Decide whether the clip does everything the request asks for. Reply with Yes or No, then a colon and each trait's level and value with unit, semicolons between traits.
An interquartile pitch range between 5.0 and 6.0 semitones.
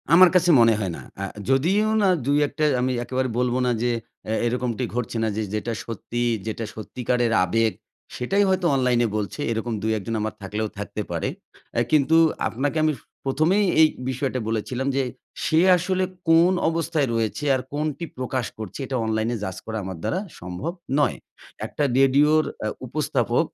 Yes: wide, 5.4 semitones